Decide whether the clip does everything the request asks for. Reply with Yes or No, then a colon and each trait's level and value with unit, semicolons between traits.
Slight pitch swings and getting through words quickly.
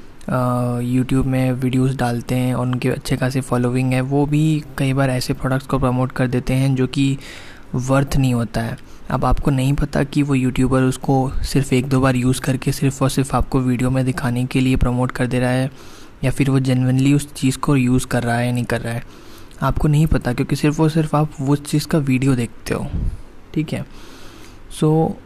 Yes: narrow, 1.7 semitones; fast, 215 wpm